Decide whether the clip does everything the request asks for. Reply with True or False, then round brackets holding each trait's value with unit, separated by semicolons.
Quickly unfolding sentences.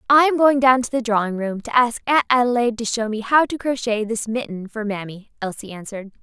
True (230 wpm)